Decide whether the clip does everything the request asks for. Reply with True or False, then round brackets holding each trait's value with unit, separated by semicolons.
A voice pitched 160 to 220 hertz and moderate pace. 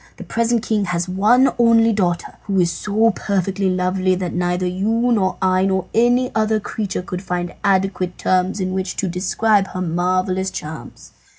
True (190 Hz; 170 wpm)